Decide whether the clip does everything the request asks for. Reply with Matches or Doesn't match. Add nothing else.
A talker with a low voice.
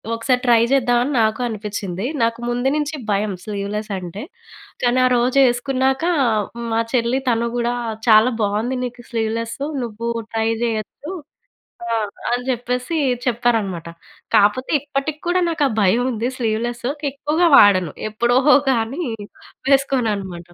Doesn't match